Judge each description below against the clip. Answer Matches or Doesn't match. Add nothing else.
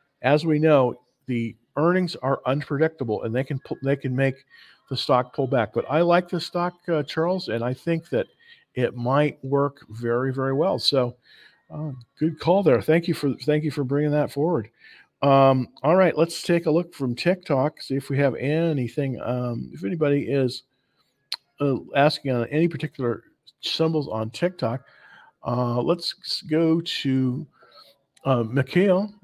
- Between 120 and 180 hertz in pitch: Matches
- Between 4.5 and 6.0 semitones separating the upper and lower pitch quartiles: Doesn't match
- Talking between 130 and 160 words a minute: Doesn't match